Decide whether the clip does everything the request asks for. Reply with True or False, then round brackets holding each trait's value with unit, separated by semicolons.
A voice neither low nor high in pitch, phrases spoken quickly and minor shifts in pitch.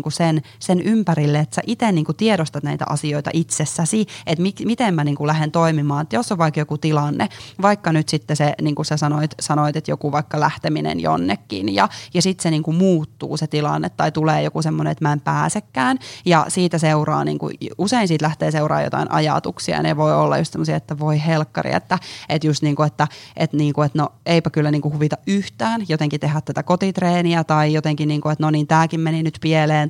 True (155 Hz; 215 wpm; 2.0 semitones)